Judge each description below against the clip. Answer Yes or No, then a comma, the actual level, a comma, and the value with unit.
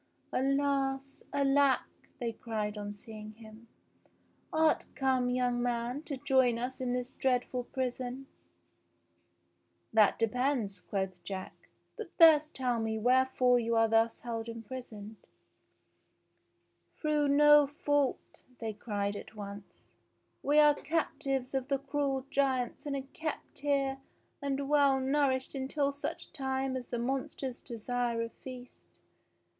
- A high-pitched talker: Yes, very high, 260 Hz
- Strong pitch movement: No, average, 3.2 semitones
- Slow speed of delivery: Yes, slow, 130 wpm